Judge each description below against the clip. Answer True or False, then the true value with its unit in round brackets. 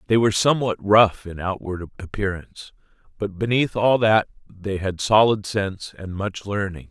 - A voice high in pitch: False (100 Hz)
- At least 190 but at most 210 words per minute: False (155 wpm)